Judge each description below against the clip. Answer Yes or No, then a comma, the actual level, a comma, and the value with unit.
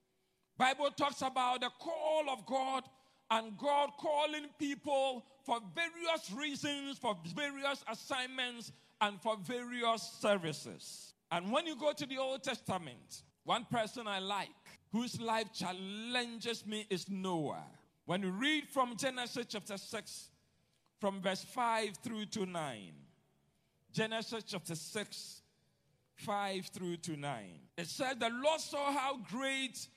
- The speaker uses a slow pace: Yes, slow, 130 wpm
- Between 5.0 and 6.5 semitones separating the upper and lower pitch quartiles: Yes, average, 5.3 semitones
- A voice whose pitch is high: Yes, high, 230 Hz